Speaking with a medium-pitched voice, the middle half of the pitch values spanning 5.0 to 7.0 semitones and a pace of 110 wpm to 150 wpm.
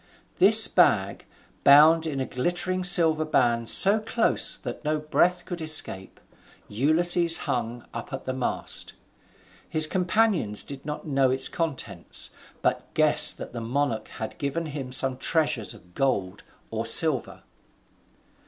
Yes: medium, 145 Hz; average, 5.3 semitones; average, 140 wpm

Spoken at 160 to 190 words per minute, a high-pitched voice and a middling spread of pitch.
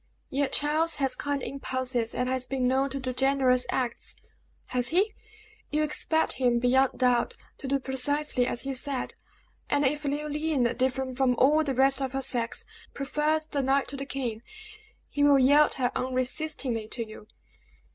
No: average, 165 wpm; very high, 270 Hz; narrow, 2.2 semitones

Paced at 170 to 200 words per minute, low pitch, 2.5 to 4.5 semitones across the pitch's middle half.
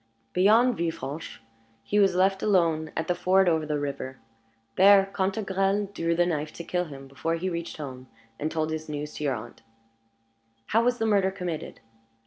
No: average, 175 wpm; medium, 170 Hz; average, 4.2 semitones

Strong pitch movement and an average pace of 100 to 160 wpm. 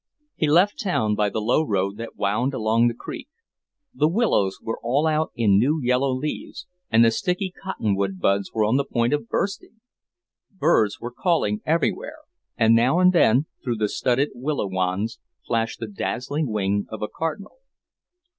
No: wide, 6.6 semitones; average, 175 wpm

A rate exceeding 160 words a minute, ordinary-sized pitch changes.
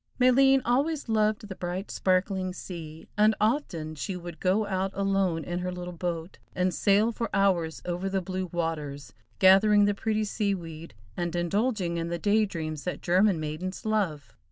Yes: average, 170 wpm; average, 3.6 semitones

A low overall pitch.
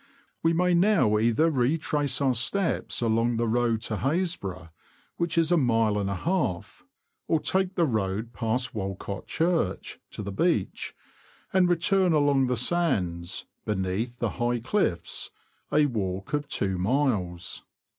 Yes: low, 120 Hz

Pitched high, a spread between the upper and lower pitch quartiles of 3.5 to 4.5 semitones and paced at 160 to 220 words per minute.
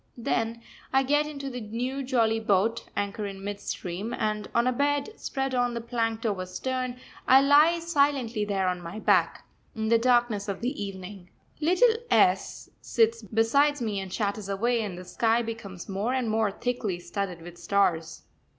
Yes: high, 225 Hz; average, 4.1 semitones; average, 175 wpm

